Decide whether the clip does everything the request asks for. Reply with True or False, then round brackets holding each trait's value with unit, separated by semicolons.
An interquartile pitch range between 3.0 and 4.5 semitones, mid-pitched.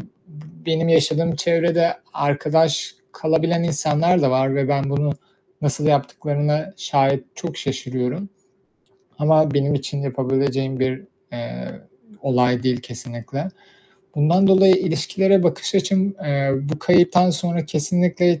True (3.9 semitones; 150 Hz)